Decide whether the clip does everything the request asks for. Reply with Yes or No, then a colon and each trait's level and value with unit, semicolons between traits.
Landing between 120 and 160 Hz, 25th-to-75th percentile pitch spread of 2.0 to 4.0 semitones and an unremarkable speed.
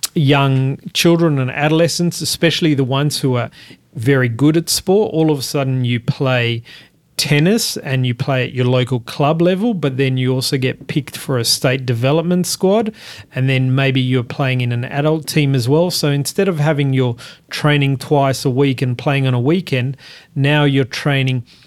Yes: medium, 140 Hz; average, 3.2 semitones; average, 185 wpm